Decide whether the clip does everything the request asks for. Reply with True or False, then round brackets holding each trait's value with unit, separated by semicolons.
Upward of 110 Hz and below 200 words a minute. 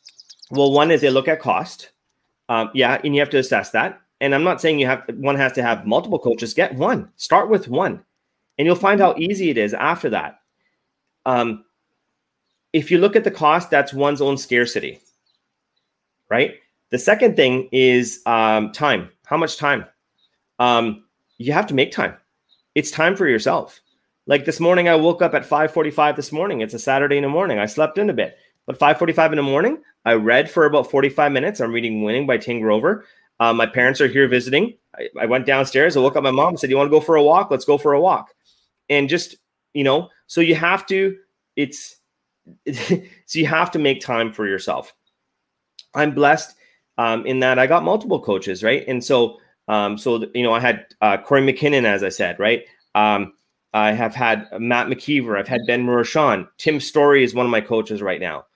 False (135 Hz; 205 wpm)